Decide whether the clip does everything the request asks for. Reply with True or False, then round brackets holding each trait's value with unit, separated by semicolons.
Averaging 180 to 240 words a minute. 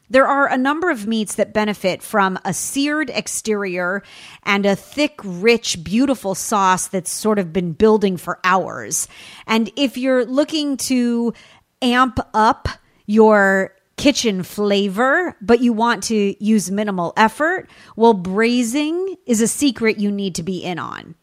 False (150 wpm)